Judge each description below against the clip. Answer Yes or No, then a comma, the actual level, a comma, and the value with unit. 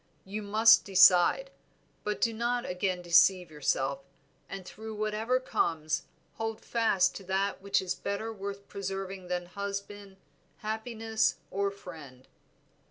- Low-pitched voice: No, high, 200 Hz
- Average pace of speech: No, slow, 125 wpm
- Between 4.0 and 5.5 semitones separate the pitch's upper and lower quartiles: No, average, 3.1 semitones